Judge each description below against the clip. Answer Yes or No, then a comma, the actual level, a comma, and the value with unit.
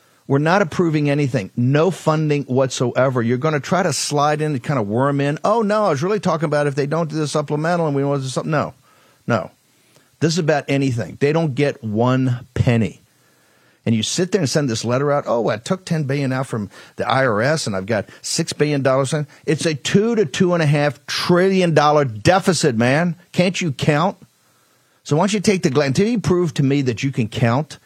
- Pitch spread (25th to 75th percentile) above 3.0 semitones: Yes, average, 4.1 semitones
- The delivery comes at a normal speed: No, fast, 225 wpm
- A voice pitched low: No, medium, 145 Hz